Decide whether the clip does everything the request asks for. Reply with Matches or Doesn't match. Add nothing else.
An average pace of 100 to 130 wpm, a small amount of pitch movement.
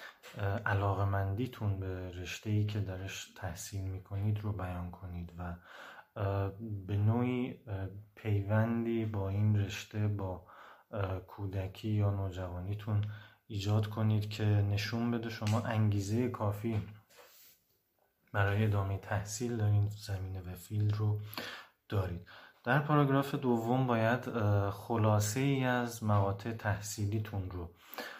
Matches